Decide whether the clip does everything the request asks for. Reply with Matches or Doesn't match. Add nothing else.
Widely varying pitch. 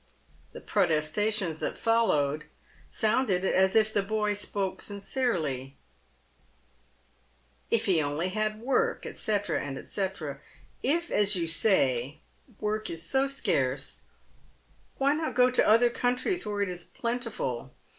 Matches